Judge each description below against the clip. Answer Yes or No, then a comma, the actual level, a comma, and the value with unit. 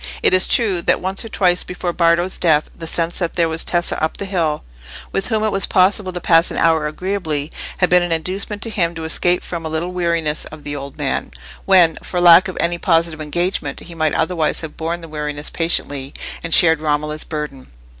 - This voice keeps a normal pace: No, fast, 215 wpm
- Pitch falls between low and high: Yes, medium, 170 Hz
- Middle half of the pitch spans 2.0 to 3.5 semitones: Yes, narrow, 2.5 semitones